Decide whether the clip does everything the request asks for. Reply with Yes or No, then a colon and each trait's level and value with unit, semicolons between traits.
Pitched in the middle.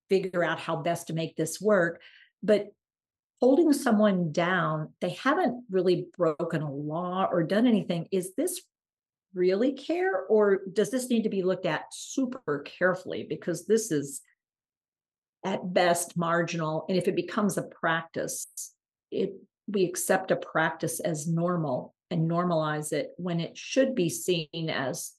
Yes: medium, 180 Hz